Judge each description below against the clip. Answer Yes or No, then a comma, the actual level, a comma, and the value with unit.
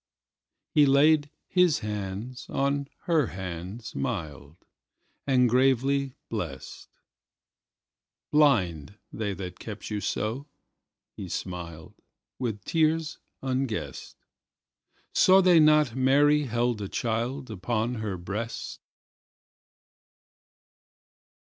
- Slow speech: Yes, slow, 75 wpm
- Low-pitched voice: Yes, low, 120 Hz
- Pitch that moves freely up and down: Yes, wide, 6.1 semitones